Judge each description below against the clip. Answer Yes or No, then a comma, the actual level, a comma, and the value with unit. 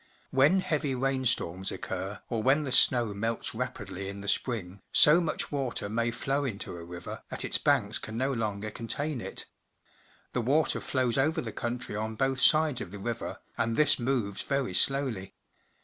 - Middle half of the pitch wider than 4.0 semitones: Yes, average, 4.9 semitones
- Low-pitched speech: Yes, low, 120 Hz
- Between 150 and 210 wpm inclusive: Yes, average, 175 wpm